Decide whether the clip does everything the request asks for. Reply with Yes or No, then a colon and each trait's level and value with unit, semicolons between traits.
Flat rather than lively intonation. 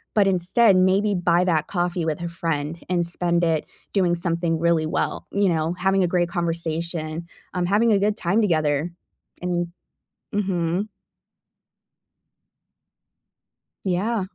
Yes: narrow, 2.2 semitones